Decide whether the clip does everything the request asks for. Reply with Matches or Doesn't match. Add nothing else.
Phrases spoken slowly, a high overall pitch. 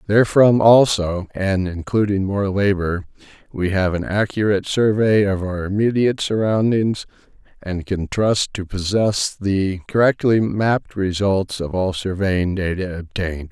Doesn't match